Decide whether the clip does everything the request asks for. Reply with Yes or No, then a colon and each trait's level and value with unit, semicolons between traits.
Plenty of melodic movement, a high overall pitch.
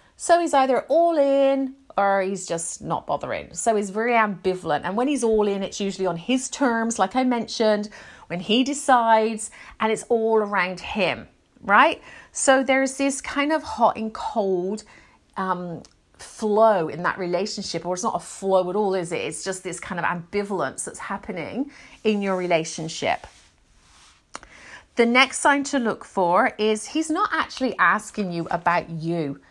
Yes: wide, 5.7 semitones; high, 215 Hz